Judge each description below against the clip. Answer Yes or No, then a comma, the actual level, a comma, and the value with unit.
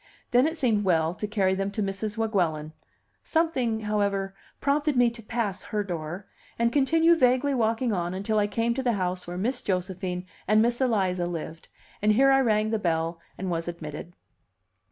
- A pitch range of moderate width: Yes, average, 4.7 semitones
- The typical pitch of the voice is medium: No, high, 210 Hz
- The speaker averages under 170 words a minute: No, average, 180 wpm